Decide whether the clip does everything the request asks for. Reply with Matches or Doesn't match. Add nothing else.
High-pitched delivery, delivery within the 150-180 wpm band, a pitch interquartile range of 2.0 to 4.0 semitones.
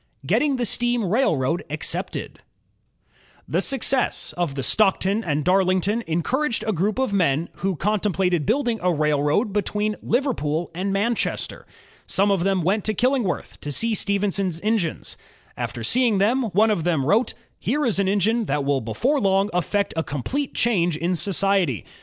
Doesn't match